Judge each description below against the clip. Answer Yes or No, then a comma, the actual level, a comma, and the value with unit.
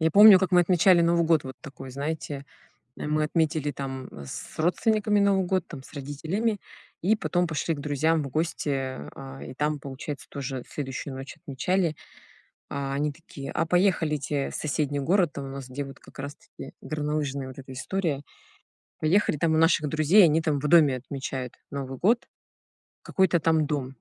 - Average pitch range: Yes, average, 3.7 semitones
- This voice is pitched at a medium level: Yes, medium, 150 Hz